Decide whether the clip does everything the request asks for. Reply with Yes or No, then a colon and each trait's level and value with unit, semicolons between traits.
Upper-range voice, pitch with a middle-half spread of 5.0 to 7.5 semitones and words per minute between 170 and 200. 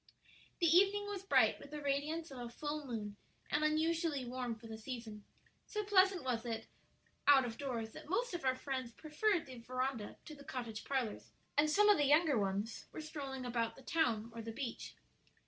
Yes: very high, 270 Hz; average, 5.3 semitones; average, 195 wpm